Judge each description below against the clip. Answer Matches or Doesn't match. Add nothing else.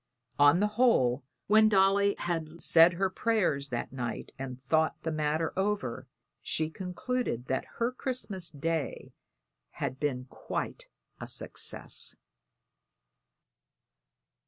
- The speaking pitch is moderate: Matches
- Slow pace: Matches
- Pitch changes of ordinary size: Doesn't match